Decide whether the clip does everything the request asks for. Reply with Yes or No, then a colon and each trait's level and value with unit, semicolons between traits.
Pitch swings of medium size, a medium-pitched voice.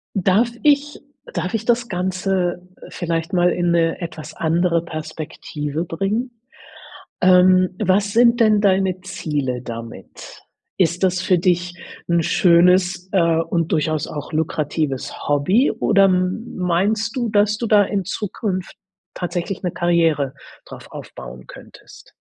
Yes: average, 3.1 semitones; medium, 180 Hz